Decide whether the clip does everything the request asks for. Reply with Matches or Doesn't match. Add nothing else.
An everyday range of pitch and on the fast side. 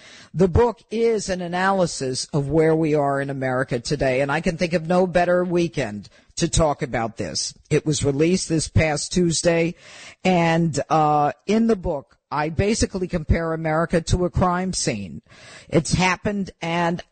Doesn't match